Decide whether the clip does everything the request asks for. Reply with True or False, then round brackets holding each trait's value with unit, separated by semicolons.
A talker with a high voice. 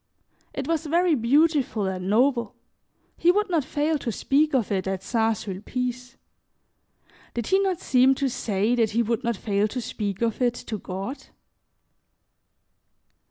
True (240 Hz)